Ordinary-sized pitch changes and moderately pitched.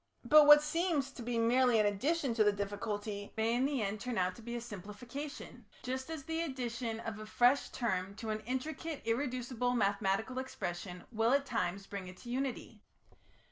No: average, 4.2 semitones; high, 235 Hz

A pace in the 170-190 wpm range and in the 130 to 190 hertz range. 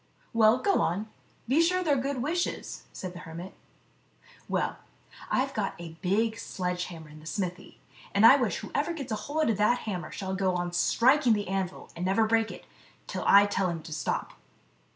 No: average, 185 wpm; high, 205 Hz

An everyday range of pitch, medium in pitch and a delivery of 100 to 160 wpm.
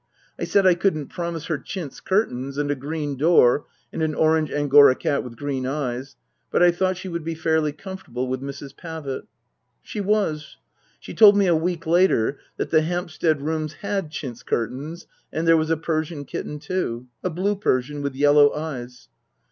No: average, 3.6 semitones; medium, 155 Hz; average, 180 wpm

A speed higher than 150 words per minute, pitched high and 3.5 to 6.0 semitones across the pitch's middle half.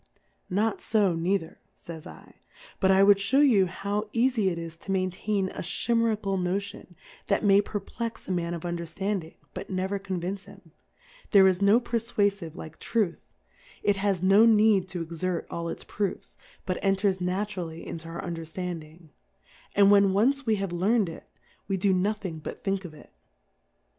No: average, 175 wpm; high, 195 Hz; average, 2.8 semitones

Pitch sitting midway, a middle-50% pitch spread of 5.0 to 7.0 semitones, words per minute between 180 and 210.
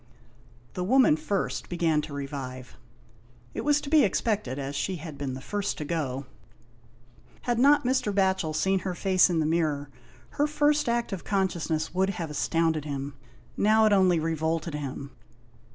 No: medium, 170 Hz; average, 5.3 semitones; average, 165 wpm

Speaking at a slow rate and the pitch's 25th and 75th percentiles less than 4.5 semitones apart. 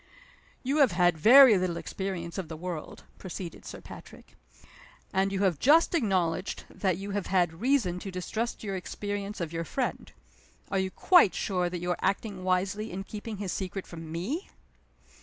No: average, 175 wpm; average, 2.8 semitones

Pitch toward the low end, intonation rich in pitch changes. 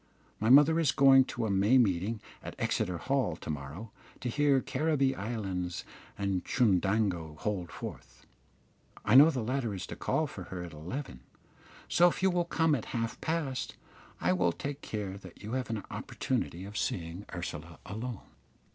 Yes: low, 110 Hz; wide, 6.7 semitones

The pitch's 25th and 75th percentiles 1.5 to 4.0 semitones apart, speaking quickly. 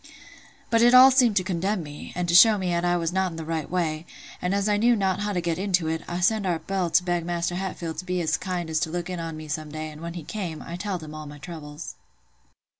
Yes: average, 2.9 semitones; fast, 265 wpm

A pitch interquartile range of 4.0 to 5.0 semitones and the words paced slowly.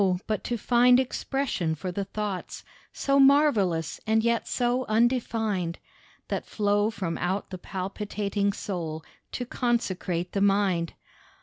Yes: average, 4.5 semitones; slow, 125 wpm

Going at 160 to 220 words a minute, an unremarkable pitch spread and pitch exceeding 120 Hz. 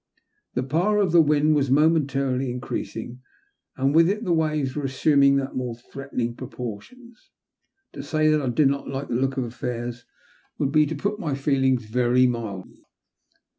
Yes: average, 165 wpm; average, 3.4 semitones; low, 135 Hz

